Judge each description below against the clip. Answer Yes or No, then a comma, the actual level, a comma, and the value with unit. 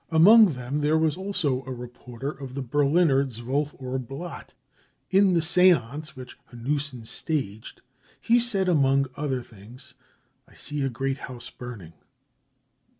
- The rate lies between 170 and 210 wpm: No, average, 155 wpm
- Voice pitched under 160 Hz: Yes, medium, 140 Hz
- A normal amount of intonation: Yes, average, 4.1 semitones